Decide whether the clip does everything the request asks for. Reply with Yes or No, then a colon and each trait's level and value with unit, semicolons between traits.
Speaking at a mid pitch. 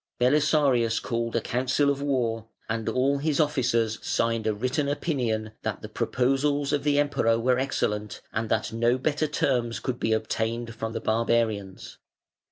No: low, 120 Hz